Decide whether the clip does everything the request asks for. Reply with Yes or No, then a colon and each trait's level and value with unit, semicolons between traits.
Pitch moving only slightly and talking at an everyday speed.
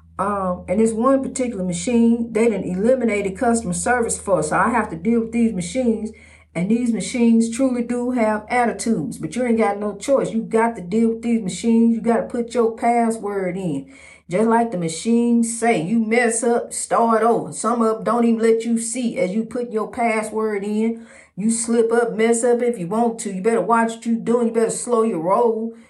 No: narrow, 1.3 semitones; fast, 215 wpm